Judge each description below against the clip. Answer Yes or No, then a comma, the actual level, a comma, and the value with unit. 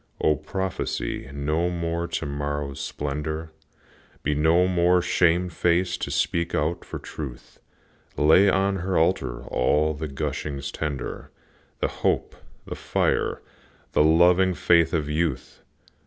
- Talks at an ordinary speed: No, slow, 125 wpm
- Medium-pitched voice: No, very low, 80 Hz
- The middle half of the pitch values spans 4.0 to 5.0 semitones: No, average, 3.1 semitones